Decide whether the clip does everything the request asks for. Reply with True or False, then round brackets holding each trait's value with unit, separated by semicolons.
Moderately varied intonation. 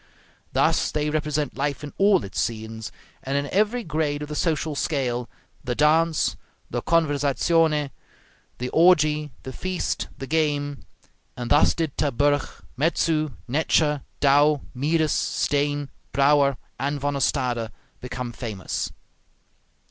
False (2.3 semitones)